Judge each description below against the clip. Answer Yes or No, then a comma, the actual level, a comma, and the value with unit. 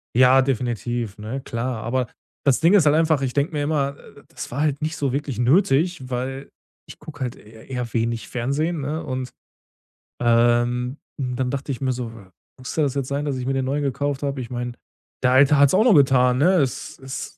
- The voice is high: No, low, 135 Hz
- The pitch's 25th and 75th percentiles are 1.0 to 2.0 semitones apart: No, narrow, 2.6 semitones